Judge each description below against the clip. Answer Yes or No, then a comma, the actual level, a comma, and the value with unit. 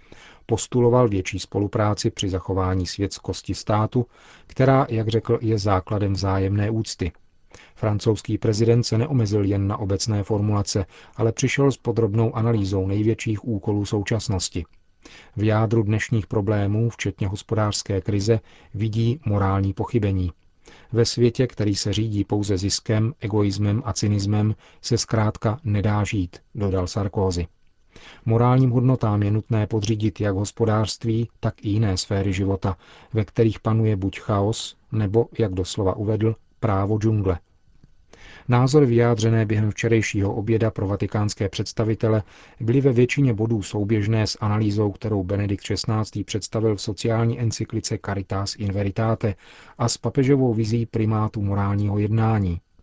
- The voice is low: Yes, low, 110 Hz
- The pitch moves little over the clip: Yes, narrow, 2.2 semitones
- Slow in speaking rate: No, average, 125 wpm